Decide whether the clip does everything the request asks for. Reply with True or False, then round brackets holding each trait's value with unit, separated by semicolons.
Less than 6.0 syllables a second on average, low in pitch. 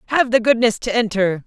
False (5.7 syllables/s; 225 Hz)